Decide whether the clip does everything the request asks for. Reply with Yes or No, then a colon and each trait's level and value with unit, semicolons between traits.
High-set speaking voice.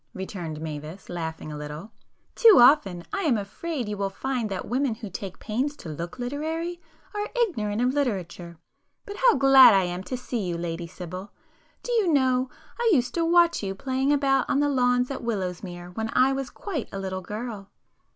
Yes: high, 235 Hz